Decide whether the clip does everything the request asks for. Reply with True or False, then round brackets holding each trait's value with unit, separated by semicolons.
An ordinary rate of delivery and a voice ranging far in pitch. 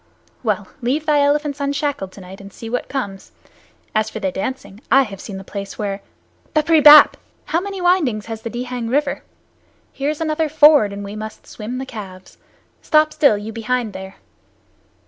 True (175 wpm; 6.3 semitones)